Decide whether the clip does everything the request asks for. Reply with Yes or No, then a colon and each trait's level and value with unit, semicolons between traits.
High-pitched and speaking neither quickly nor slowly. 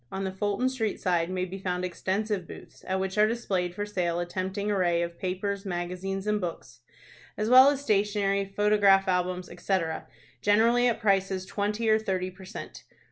Yes: high, 195 Hz; average, 180 wpm